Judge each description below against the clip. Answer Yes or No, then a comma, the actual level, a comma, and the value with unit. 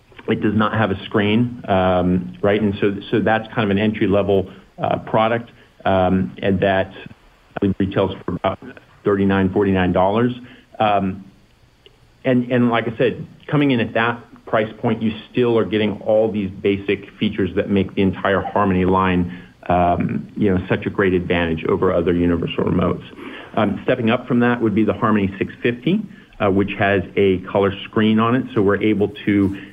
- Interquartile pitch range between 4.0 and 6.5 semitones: No, average, 2.8 semitones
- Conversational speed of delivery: Yes, average, 180 wpm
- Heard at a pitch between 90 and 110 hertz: Yes, low, 100 Hz